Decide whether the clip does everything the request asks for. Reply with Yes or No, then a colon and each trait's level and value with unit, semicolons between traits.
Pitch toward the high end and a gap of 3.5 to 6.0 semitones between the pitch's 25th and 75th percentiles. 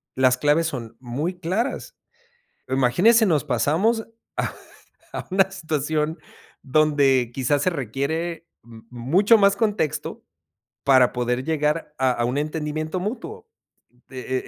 No: medium, 150 Hz; wide, 5.5 semitones